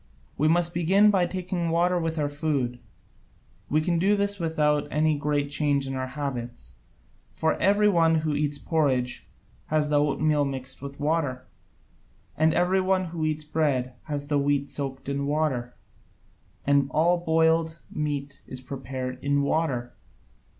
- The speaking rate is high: No, average, 150 wpm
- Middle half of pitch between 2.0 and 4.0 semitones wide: Yes, average, 2.8 semitones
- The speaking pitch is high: No, medium, 150 Hz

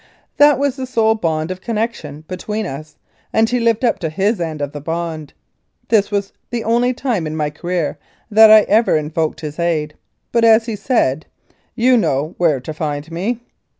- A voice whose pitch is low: No, medium, 185 Hz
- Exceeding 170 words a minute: Yes, average, 185 wpm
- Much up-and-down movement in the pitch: Yes, wide, 6.6 semitones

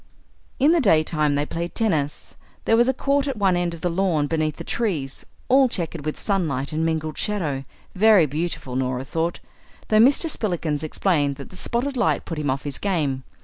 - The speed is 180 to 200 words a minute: Yes, average, 190 wpm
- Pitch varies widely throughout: Yes, wide, 6.2 semitones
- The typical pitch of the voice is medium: Yes, medium, 165 Hz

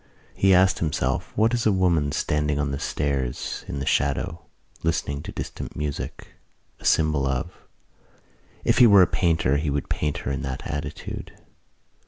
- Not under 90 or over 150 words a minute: No, average, 165 wpm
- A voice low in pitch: Yes, very low, 75 Hz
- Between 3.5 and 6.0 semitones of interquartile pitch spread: Yes, average, 3.9 semitones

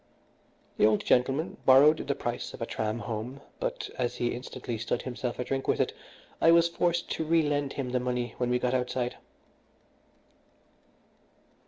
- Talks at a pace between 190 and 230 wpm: No, average, 165 wpm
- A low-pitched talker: Yes, low, 125 Hz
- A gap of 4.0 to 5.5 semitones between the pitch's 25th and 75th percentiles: No, average, 2.9 semitones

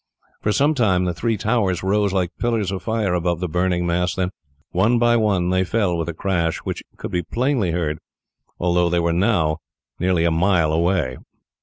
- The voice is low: Yes, very low, 90 Hz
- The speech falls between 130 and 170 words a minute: No, average, 190 wpm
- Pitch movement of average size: Yes, average, 3.3 semitones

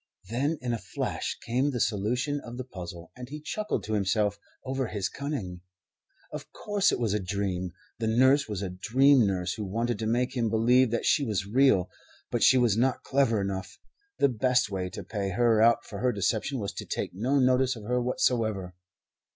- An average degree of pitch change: Yes, average, 4.3 semitones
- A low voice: Yes, low, 115 Hz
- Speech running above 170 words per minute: Yes, average, 200 wpm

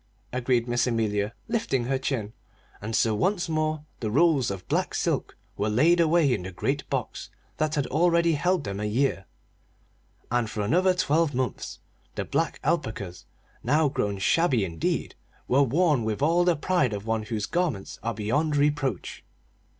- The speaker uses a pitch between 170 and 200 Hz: No, low, 130 Hz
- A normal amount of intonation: No, wide, 6.7 semitones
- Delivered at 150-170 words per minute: Yes, average, 165 wpm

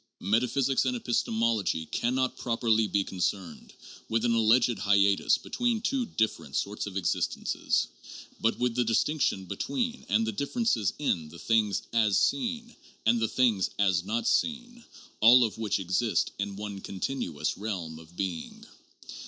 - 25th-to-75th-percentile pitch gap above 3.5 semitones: Yes, average, 4.3 semitones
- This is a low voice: Yes, low, 110 Hz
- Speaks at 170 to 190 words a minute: No, average, 155 wpm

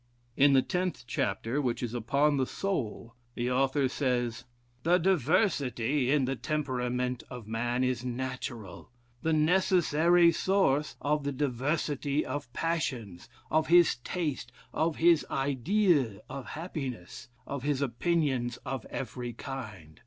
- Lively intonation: No, average, 4.2 semitones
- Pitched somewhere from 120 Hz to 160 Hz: Yes, low, 135 Hz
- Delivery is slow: Yes, slow, 130 wpm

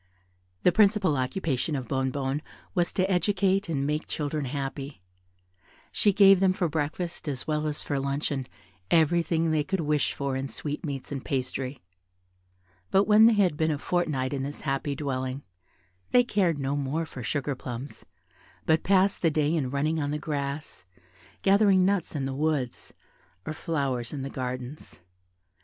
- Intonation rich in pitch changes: No, average, 4.1 semitones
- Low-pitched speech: No, medium, 150 Hz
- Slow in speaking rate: No, average, 160 wpm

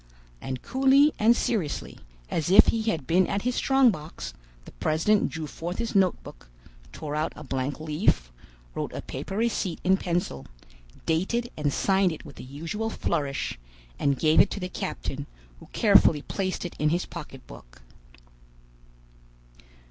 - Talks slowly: No, average, 155 wpm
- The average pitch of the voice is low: No, medium, 170 Hz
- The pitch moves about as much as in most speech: No, wide, 5.7 semitones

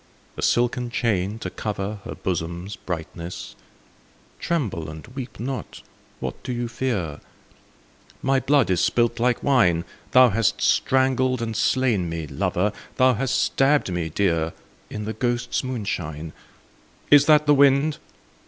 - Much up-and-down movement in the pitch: Yes, wide, 6.4 semitones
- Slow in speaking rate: No, average, 145 wpm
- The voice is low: Yes, low, 115 Hz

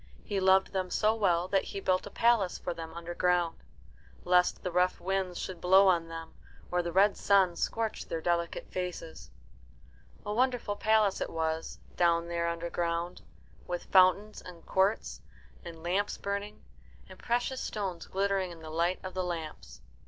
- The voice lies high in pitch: No, medium, 180 Hz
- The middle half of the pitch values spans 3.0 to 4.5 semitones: No, narrow, 2.6 semitones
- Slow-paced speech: No, average, 160 wpm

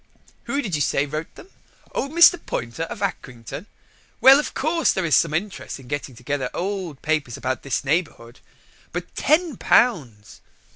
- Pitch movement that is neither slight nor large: No, wide, 8.6 semitones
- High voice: No, medium, 155 Hz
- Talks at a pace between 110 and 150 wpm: No, average, 160 wpm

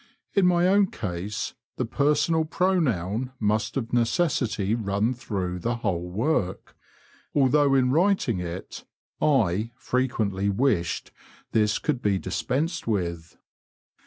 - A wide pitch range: Yes, wide, 6.7 semitones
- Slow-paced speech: Yes, slow, 120 wpm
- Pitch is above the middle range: No, low, 115 Hz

